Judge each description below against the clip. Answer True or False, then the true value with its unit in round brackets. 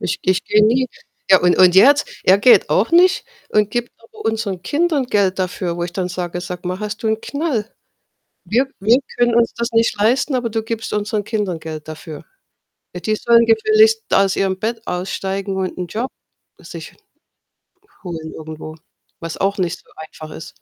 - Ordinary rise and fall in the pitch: True (4.5 semitones)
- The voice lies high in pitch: True (205 Hz)